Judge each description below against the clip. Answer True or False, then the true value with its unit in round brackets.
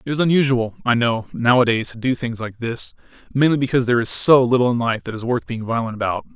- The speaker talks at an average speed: False (225 wpm)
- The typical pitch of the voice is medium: False (120 Hz)